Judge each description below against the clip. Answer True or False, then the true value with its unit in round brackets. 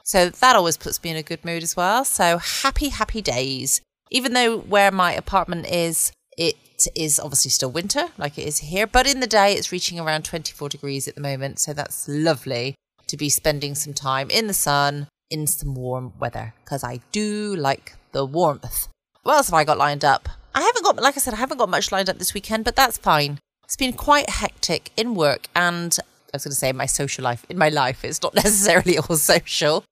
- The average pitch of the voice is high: False (165 Hz)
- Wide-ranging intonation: True (6.3 semitones)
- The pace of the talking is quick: True (220 wpm)